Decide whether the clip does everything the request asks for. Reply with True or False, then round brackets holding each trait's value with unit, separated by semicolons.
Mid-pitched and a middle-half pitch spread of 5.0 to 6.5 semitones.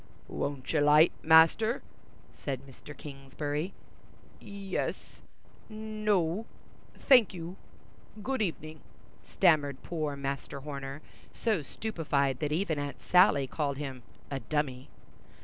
True (155 Hz; 5.3 semitones)